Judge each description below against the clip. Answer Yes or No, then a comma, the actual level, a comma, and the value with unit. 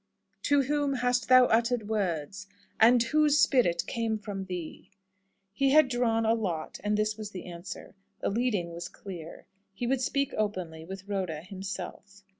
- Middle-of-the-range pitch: No, high, 215 Hz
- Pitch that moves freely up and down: No, average, 4.8 semitones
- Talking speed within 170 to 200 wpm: No, average, 160 wpm